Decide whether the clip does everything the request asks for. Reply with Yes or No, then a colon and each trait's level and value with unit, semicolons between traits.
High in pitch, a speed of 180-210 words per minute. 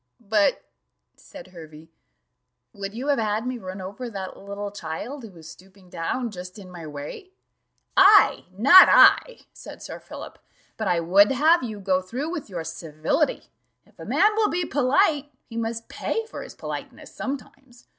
No: high, 215 Hz; average, 165 wpm